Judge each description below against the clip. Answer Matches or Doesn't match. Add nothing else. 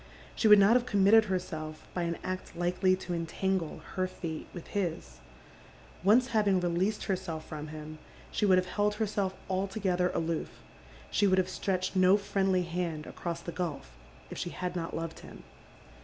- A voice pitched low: Doesn't match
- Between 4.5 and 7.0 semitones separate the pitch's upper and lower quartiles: Doesn't match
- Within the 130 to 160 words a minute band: Doesn't match